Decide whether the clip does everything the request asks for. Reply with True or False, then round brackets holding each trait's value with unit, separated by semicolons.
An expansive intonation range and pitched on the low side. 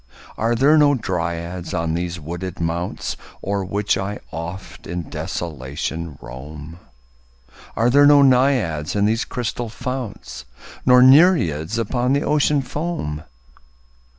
True (7.4 semitones; 100 Hz)